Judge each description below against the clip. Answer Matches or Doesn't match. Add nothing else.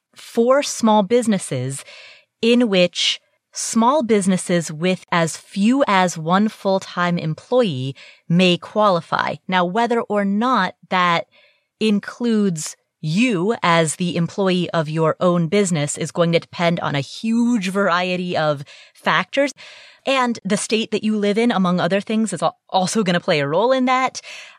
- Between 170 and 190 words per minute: Doesn't match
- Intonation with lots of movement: Doesn't match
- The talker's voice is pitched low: Doesn't match